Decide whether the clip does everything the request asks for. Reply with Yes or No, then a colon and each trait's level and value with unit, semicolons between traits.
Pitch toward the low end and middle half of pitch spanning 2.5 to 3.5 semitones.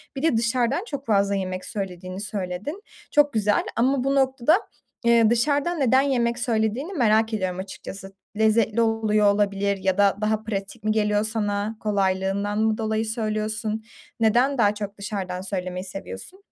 No: high, 215 Hz; average, 2.9 semitones